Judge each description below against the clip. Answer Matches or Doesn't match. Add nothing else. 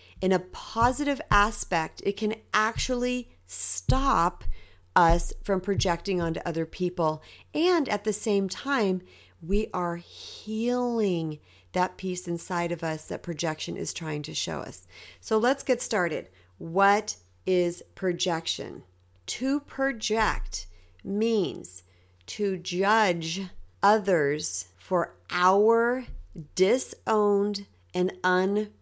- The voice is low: Doesn't match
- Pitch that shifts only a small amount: Doesn't match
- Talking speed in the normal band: Doesn't match